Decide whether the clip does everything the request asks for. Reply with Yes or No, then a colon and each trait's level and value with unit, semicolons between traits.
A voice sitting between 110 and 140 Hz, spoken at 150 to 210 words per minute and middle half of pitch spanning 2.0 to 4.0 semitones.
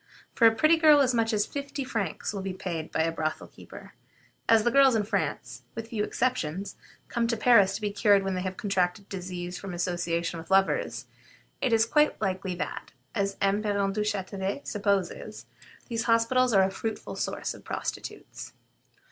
No: high, 200 Hz; average, 180 wpm; average, 3.6 semitones